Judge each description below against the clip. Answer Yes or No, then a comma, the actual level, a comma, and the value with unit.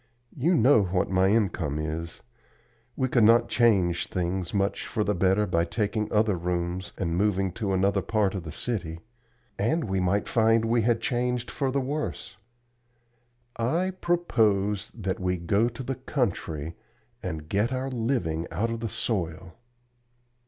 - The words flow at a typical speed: Yes, average, 160 wpm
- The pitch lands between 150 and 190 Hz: No, low, 105 Hz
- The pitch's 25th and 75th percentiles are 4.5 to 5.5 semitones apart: Yes, average, 4.8 semitones